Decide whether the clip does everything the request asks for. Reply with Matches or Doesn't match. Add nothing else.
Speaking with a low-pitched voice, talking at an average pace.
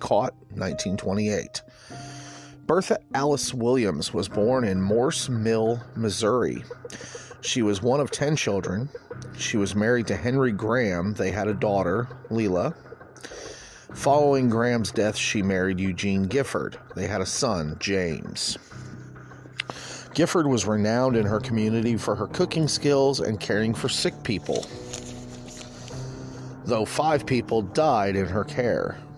Doesn't match